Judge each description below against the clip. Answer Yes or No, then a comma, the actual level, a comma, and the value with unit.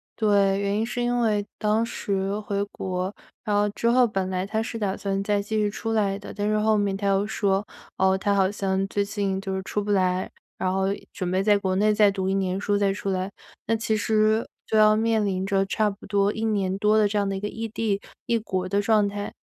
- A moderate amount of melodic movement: No, narrow, 1.7 semitones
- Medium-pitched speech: No, high, 205 Hz